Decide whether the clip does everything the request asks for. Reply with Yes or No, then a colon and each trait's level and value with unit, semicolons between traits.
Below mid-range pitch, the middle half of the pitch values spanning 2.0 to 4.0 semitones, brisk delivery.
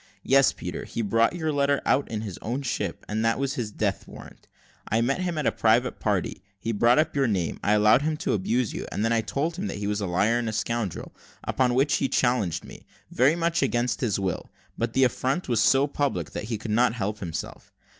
No: low, 120 Hz; average, 4.4 semitones; fast, 225 wpm